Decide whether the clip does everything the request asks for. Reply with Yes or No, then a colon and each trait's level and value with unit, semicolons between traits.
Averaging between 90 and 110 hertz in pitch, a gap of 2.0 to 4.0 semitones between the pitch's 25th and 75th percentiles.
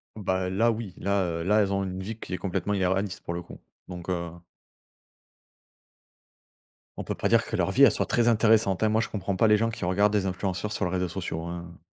Yes: very low, 95 Hz; average, 2.8 semitones